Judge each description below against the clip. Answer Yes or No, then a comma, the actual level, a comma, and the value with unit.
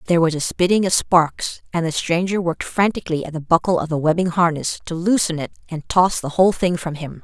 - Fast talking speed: Yes, fast, 230 wpm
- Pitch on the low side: No, medium, 170 Hz